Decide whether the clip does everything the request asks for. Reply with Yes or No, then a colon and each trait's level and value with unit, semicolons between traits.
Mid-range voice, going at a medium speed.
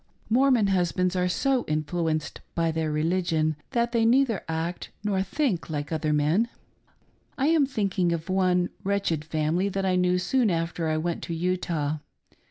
Yes: medium, 180 Hz; average, 160 wpm